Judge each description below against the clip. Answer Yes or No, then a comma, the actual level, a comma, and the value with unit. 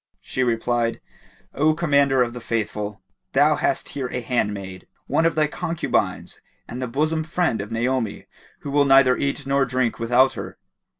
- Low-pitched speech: Yes, low, 130 Hz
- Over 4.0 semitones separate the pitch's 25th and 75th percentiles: No, average, 3.6 semitones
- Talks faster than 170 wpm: No, average, 165 wpm